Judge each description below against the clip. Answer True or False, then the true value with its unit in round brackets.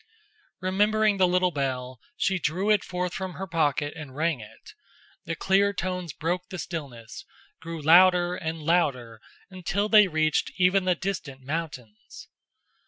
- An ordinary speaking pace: True (145 wpm)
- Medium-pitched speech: True (170 Hz)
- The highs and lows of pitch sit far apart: False (3.8 semitones)